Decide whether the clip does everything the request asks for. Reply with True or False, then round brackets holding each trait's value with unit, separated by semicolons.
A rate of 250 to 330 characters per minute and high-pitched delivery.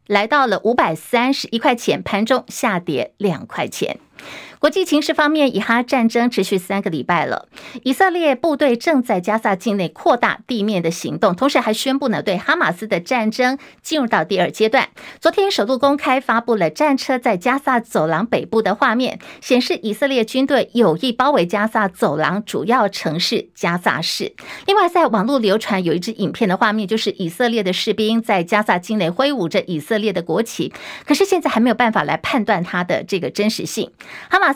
True (300 characters per minute; 225 Hz)